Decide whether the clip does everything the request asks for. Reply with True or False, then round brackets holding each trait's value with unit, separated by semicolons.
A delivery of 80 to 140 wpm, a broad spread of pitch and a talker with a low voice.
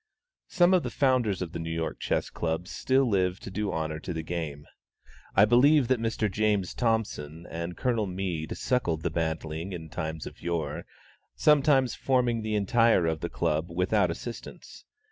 False (170 wpm; 6.3 semitones; 95 Hz)